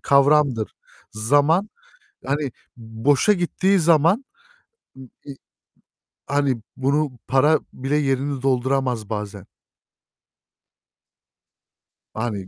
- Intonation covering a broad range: No, average, 3.6 semitones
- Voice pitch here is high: No, low, 135 Hz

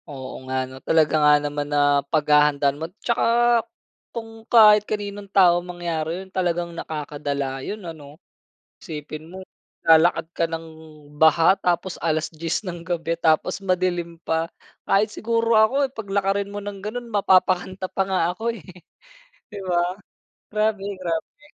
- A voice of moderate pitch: Yes, medium, 175 Hz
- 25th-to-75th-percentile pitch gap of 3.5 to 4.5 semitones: Yes, average, 4.2 semitones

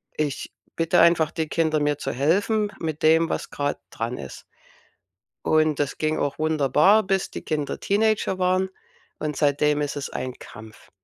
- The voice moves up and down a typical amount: Yes, average, 3.1 semitones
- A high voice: No, medium, 155 Hz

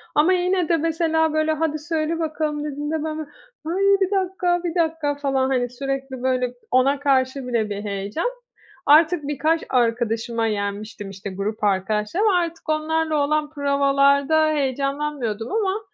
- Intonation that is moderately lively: Yes, average, 4.4 semitones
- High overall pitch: Yes, very high, 290 Hz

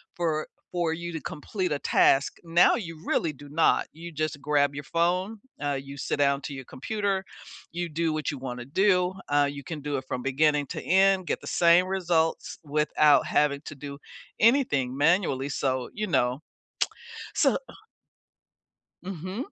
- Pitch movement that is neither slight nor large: Yes, average, 3.8 semitones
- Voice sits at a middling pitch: Yes, medium, 155 Hz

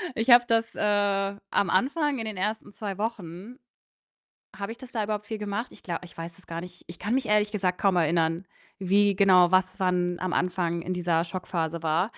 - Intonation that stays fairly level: No, average, 3.1 semitones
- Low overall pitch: No, high, 195 Hz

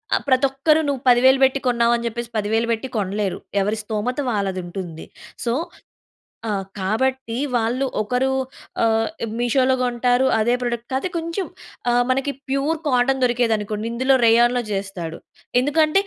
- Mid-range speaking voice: No, high, 240 Hz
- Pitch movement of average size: Yes, average, 3.2 semitones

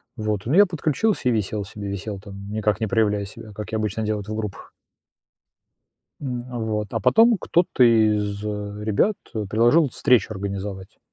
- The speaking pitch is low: Yes, low, 110 Hz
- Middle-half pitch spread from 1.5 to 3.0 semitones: Yes, average, 2.7 semitones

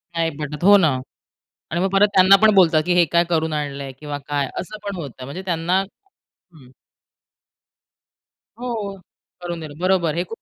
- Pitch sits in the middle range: Yes, medium, 170 Hz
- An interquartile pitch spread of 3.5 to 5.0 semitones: Yes, average, 4.1 semitones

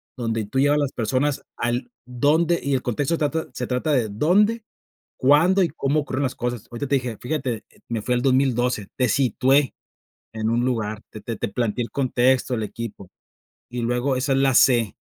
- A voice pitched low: Yes, low, 125 Hz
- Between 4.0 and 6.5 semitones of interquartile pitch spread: No, average, 3.2 semitones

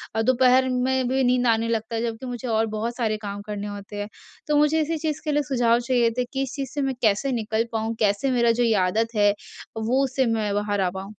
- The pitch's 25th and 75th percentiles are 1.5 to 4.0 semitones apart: Yes, average, 3.2 semitones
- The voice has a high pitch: Yes, high, 235 Hz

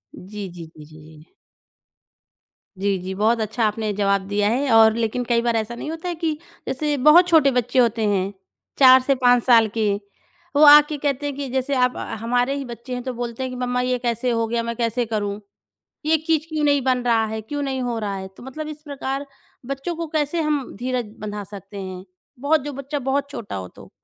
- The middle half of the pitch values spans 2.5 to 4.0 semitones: No, average, 4.6 semitones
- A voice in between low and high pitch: No, high, 245 Hz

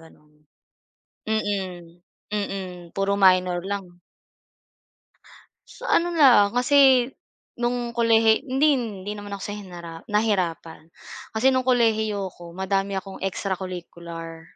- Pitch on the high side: Yes, high, 200 Hz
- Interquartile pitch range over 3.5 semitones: Yes, average, 4.1 semitones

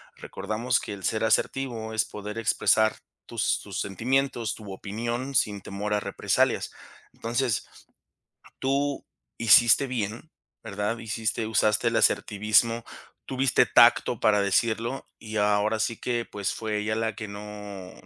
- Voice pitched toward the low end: Yes, low, 110 Hz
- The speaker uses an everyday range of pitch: No, narrow, 2.1 semitones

